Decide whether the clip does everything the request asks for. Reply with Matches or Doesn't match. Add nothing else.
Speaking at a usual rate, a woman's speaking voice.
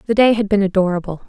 Doesn't match